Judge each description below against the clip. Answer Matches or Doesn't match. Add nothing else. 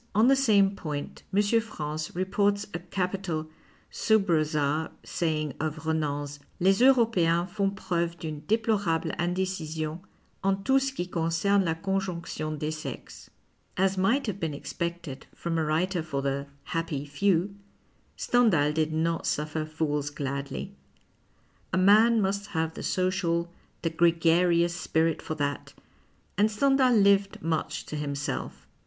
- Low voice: Doesn't match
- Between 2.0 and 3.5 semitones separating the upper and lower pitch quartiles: Doesn't match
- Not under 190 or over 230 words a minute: Doesn't match